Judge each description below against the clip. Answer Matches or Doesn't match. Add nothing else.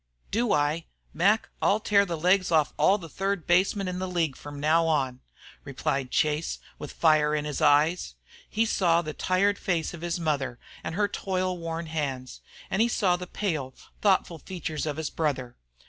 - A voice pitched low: Doesn't match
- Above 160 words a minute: Matches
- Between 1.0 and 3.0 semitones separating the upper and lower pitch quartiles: Doesn't match